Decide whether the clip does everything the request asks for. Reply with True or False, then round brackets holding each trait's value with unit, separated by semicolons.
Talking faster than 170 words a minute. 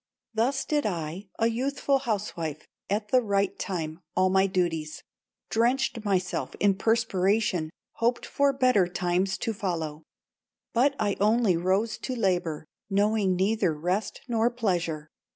False (135 wpm)